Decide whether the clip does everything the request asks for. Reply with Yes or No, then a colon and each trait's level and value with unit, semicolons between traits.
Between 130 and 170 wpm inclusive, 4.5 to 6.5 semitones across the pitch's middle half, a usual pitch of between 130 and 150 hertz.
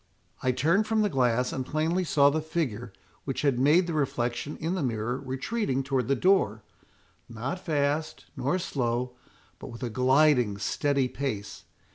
No: average, 160 wpm; average, 4.1 semitones; low, 135 Hz